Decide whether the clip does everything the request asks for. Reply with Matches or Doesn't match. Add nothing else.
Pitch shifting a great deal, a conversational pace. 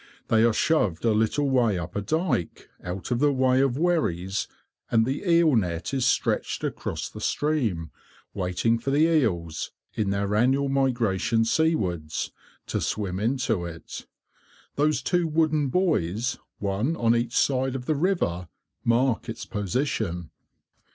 Matches